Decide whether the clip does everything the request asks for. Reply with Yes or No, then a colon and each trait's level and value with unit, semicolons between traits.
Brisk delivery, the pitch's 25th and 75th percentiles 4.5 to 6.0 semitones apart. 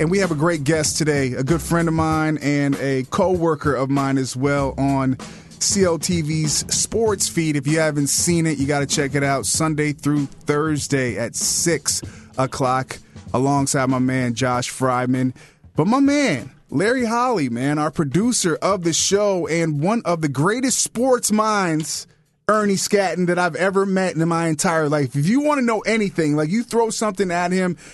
No: average, 185 wpm; average, 5.0 semitones